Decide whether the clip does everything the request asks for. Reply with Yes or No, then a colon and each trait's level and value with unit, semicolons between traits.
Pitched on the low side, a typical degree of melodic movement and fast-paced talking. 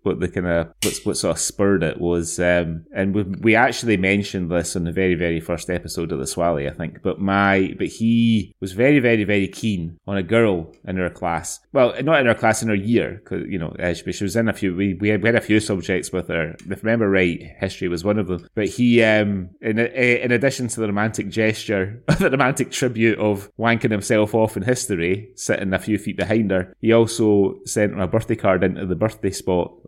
Yes: low, 105 Hz; average, 3.4 semitones; fast, 230 wpm